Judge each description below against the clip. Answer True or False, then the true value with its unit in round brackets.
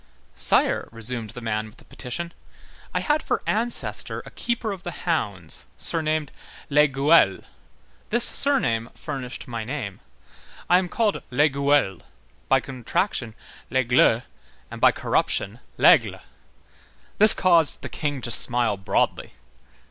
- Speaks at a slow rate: True (125 wpm)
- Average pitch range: False (6.8 semitones)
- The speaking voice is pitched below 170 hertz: True (135 Hz)